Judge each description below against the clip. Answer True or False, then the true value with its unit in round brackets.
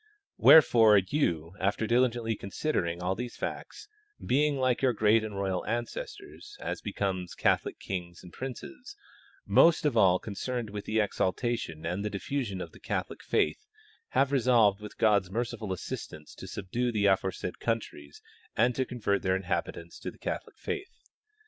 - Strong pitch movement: False (4.6 semitones)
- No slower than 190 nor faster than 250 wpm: False (155 wpm)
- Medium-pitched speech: False (110 Hz)